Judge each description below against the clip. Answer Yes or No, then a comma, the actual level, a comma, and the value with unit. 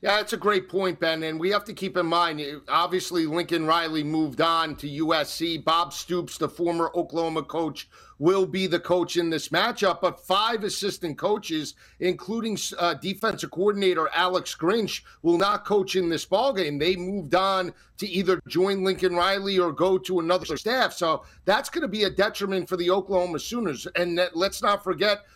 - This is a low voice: No, medium, 180 Hz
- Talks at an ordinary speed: Yes, average, 185 wpm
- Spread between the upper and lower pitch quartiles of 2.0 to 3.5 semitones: Yes, narrow, 2.6 semitones